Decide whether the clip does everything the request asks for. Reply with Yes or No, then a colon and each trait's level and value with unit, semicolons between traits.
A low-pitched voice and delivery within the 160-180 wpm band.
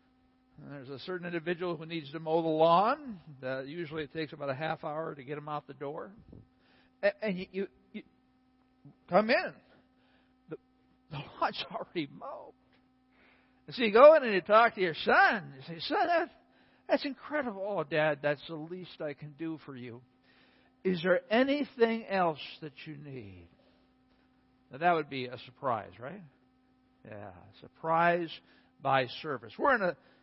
No: medium, 160 Hz; average, 165 wpm